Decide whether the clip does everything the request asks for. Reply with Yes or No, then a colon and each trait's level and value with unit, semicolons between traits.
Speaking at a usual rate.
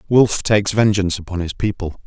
Yes: average, 175 wpm